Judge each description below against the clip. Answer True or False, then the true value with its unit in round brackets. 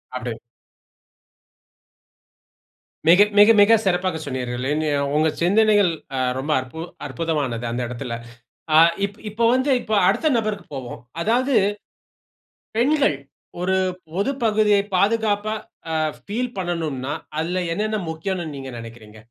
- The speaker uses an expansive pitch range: True (7.8 semitones)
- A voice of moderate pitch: True (180 Hz)